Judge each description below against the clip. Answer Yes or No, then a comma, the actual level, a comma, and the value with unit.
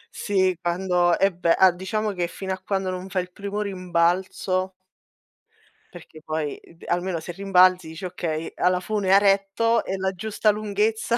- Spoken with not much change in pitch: Yes, narrow, 2.1 semitones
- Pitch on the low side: No, medium, 185 Hz